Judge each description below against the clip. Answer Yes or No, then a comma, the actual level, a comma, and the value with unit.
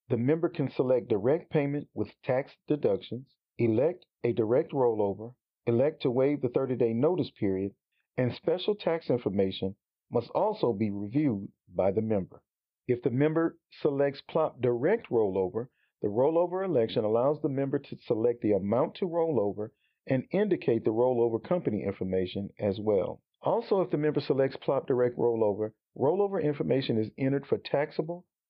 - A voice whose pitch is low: Yes, low, 125 Hz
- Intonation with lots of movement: Yes, wide, 5.8 semitones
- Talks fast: No, average, 155 wpm